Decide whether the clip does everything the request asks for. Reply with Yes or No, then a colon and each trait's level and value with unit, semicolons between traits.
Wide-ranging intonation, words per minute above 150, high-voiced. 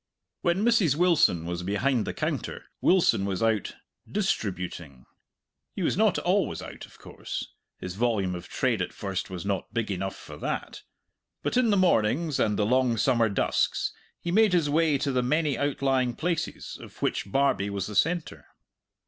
No: wide, 8.4 semitones; average, 170 wpm; low, 120 Hz